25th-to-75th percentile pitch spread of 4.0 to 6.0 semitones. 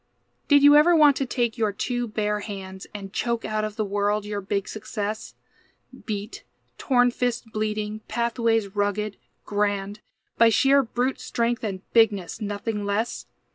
No: narrow, 2.6 semitones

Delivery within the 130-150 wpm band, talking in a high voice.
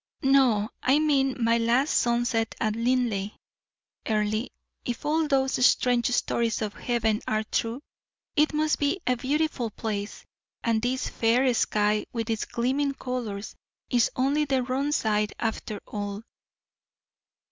Yes: slow, 135 wpm; high, 240 Hz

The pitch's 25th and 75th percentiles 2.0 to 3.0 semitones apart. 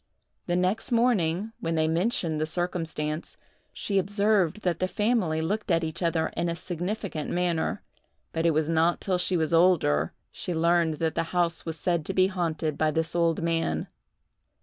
Yes: narrow, 2.4 semitones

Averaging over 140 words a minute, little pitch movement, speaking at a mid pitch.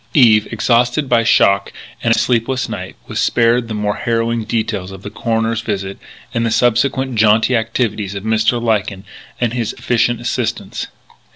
No: average, 160 wpm; narrow, 2.0 semitones; low, 115 Hz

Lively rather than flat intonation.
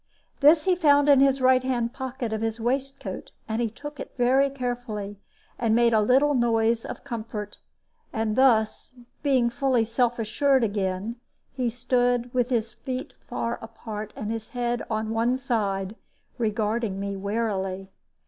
No: average, 3.0 semitones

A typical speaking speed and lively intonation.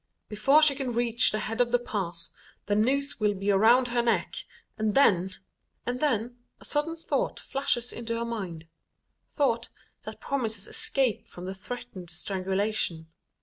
No: average, 155 wpm; average, 3.8 semitones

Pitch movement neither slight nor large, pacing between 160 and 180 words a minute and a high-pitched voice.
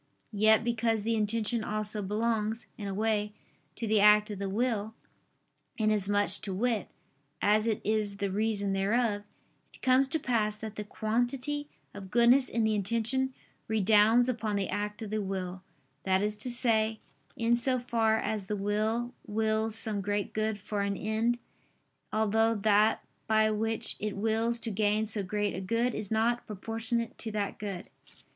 No: narrow, 1.7 semitones; average, 165 wpm; high, 215 Hz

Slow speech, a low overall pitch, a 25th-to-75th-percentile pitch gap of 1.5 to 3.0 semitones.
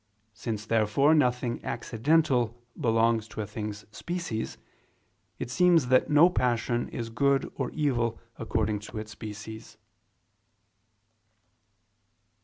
No: slow, 105 wpm; low, 115 Hz; average, 3.8 semitones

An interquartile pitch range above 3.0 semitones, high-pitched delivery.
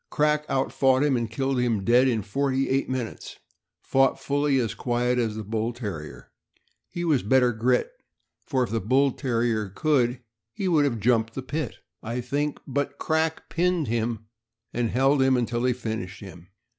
No: average, 3.4 semitones; low, 125 Hz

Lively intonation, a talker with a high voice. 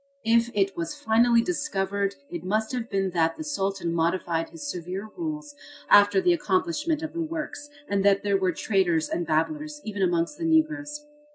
Yes: wide, 8.1 semitones; high, 215 Hz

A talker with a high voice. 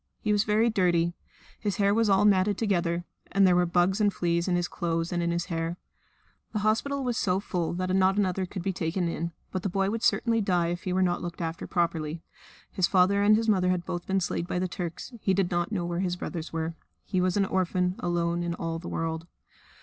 No: medium, 180 Hz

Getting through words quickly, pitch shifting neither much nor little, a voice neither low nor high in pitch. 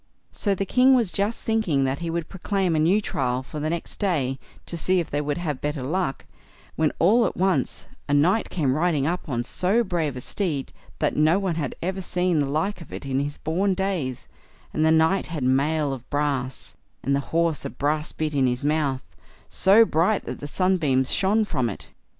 Yes: fast, 210 wpm; average, 4.9 semitones; medium, 160 Hz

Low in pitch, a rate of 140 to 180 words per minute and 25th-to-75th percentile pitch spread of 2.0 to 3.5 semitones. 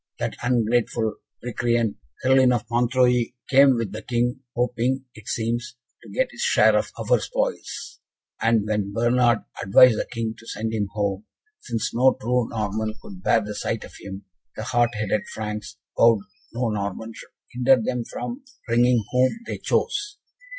Yes: low, 120 Hz; average, 160 wpm; narrow, 2.4 semitones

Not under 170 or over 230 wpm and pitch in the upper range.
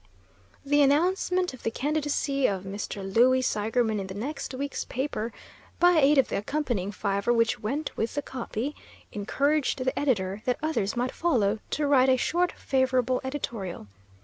No: average, 160 wpm; very high, 255 Hz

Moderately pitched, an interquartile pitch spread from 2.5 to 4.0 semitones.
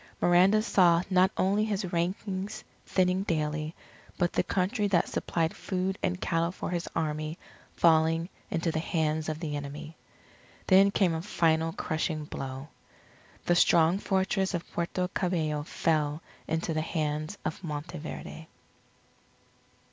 Yes: medium, 170 Hz; average, 2.9 semitones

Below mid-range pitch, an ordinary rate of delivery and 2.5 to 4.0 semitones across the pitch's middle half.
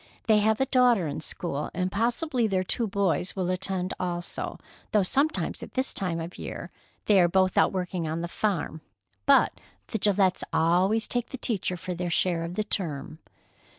No: medium, 185 Hz; average, 185 wpm; average, 3.7 semitones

